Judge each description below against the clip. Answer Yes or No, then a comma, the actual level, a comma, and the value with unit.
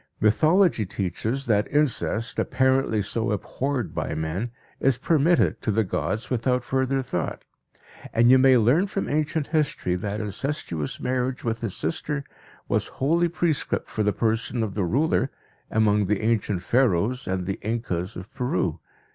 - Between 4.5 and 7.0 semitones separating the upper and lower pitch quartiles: Yes, average, 4.8 semitones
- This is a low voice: Yes, low, 115 Hz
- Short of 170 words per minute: Yes, average, 150 wpm